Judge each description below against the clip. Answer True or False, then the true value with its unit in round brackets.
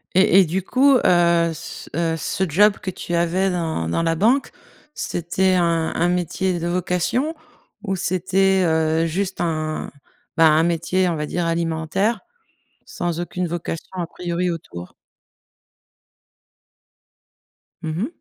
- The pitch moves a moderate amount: False (2.3 semitones)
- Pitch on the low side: False (175 Hz)